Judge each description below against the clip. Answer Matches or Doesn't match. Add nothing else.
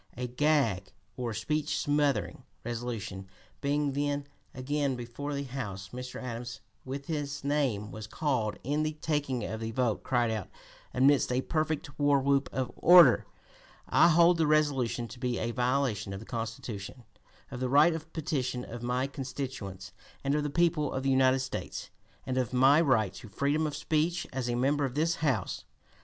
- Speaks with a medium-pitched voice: Doesn't match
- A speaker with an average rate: Matches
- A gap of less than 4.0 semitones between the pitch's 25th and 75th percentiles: Matches